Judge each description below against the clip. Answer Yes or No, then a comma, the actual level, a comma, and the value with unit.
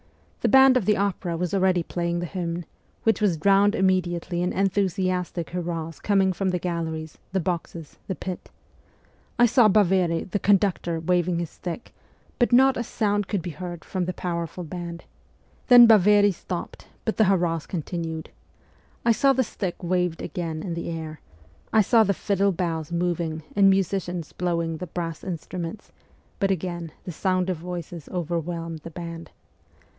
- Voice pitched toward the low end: No, medium, 180 Hz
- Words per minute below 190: Yes, average, 165 wpm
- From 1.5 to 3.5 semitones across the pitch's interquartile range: Yes, average, 2.7 semitones